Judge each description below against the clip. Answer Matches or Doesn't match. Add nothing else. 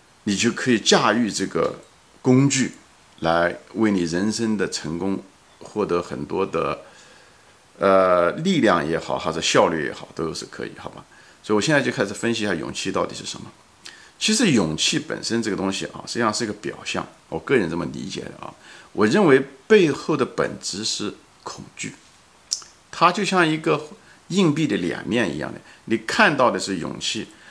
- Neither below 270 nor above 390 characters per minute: Doesn't match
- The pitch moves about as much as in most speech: Doesn't match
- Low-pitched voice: Matches